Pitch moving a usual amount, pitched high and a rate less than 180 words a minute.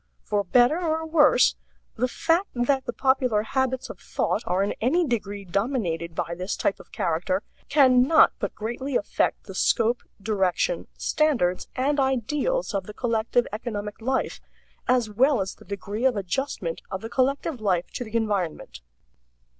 Yes: average, 5.0 semitones; high, 235 Hz; average, 160 wpm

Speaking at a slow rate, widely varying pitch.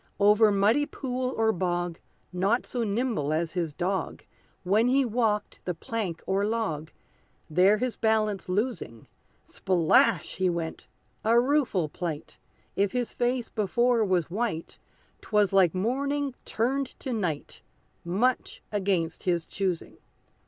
No: slow, 130 wpm; average, 5.0 semitones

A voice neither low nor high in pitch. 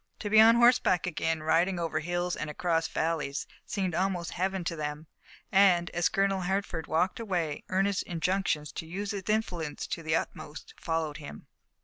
Yes: medium, 175 Hz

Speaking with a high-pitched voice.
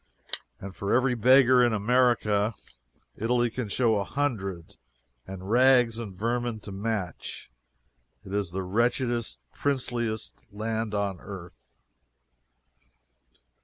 No: low, 110 Hz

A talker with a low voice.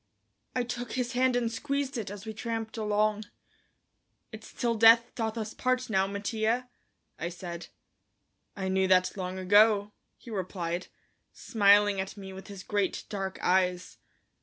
No: high, 210 Hz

